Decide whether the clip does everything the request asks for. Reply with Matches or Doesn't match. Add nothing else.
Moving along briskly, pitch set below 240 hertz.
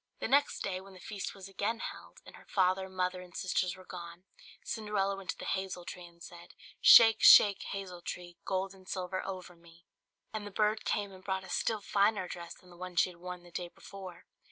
Matches